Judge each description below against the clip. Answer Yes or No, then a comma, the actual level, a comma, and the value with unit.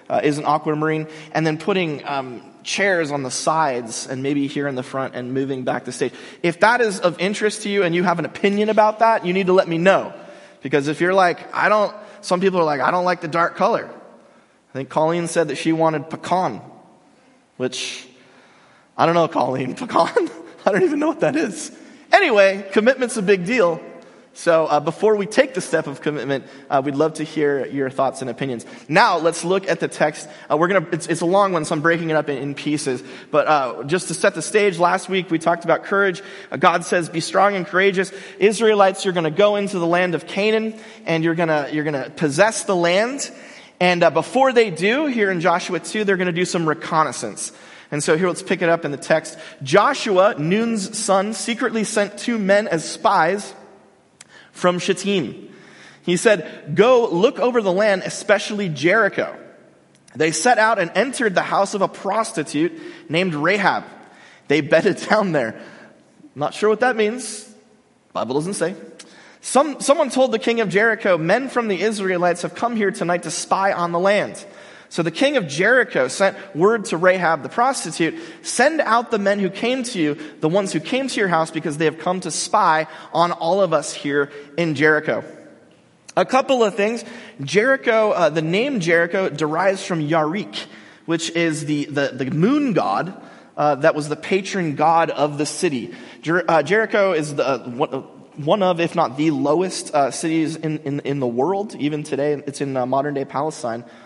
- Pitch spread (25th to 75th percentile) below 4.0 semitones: No, average, 5.0 semitones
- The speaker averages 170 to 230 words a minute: Yes, average, 195 wpm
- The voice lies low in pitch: No, medium, 175 Hz